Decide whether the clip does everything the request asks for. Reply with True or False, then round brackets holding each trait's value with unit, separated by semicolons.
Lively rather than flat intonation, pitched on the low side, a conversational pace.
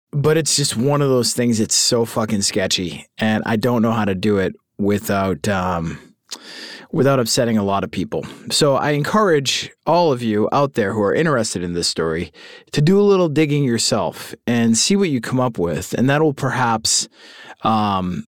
True (5.9 semitones; 115 Hz; 195 wpm)